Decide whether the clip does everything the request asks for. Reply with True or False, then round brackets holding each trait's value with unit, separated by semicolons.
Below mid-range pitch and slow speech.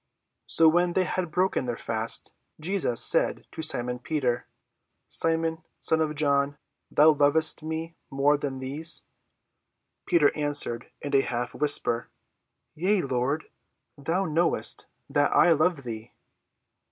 False (150 Hz; 130 wpm)